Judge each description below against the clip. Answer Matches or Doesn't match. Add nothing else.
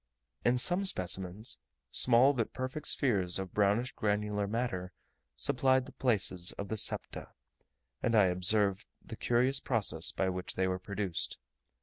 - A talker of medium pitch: Doesn't match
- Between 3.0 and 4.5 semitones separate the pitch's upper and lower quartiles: Doesn't match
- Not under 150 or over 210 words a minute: Doesn't match